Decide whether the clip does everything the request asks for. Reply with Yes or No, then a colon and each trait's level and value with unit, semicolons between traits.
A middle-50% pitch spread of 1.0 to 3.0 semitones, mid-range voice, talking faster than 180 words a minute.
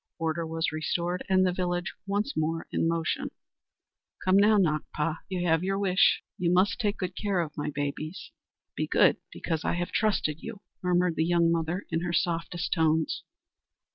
No: narrow, 2.4 semitones; medium, 175 Hz; average, 170 wpm